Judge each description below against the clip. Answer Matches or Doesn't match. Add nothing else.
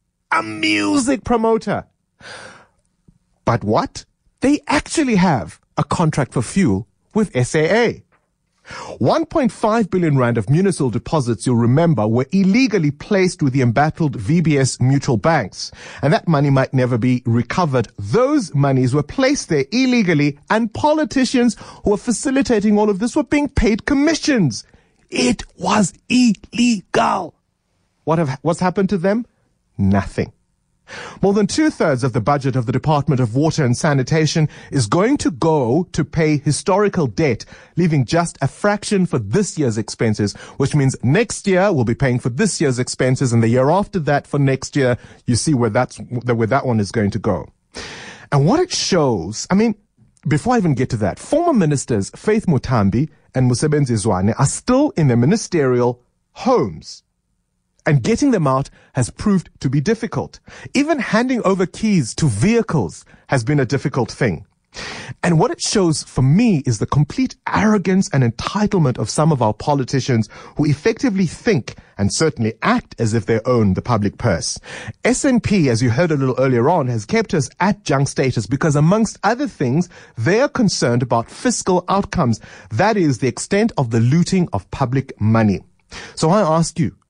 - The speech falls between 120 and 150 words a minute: Doesn't match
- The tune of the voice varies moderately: Doesn't match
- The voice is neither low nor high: Matches